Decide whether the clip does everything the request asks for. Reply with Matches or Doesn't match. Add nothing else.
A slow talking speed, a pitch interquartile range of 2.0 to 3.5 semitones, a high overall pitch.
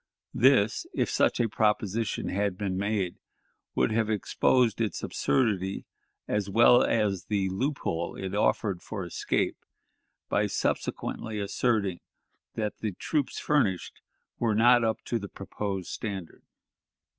Doesn't match